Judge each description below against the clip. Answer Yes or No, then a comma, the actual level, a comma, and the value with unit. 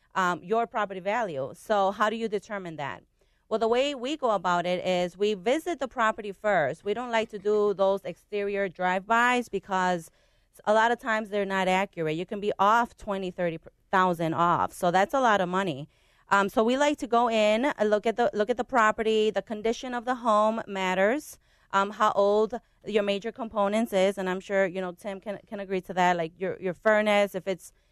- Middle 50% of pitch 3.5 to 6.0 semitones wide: No, average, 3.0 semitones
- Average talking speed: No, fast, 210 wpm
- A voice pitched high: Yes, high, 205 Hz